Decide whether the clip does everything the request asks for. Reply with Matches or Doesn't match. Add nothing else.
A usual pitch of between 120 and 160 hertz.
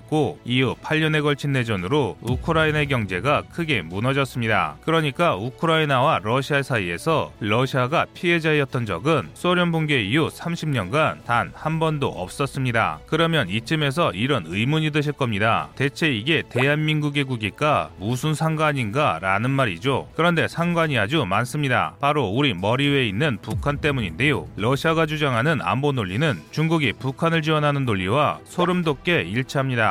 Matches